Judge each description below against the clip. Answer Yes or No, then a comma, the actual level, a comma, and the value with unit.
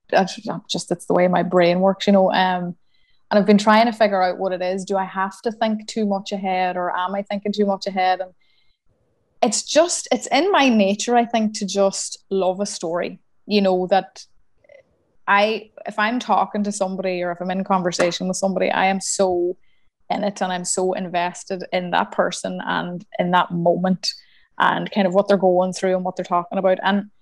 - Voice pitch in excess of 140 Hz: Yes, high, 190 Hz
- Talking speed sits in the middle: No, fast, 210 wpm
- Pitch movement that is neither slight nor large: No, narrow, 2.0 semitones